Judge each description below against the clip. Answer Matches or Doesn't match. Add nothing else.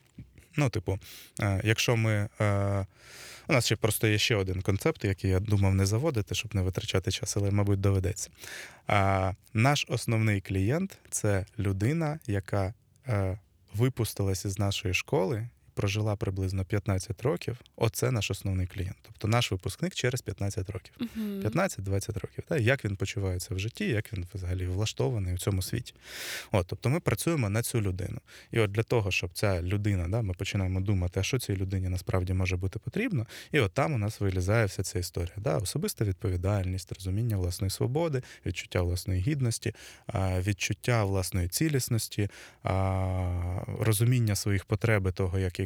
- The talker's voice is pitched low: Matches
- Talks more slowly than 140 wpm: Doesn't match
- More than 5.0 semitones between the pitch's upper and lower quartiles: Doesn't match